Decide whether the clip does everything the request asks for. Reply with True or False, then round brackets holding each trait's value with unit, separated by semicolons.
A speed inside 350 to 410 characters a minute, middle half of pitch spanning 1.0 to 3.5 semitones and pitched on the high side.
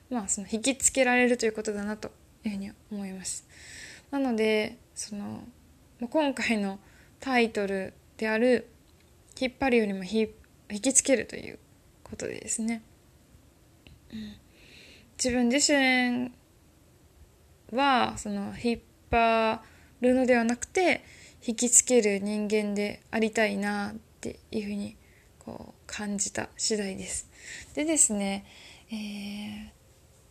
False (235 characters per minute; 3.2 semitones; 220 Hz)